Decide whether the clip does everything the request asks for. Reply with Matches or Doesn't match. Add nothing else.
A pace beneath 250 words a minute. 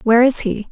Doesn't match